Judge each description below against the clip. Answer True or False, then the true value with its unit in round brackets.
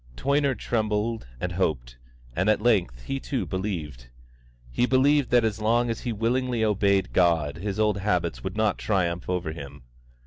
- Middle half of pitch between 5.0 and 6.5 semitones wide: True (5.4 semitones)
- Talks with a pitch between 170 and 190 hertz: False (105 Hz)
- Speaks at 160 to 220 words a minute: True (165 wpm)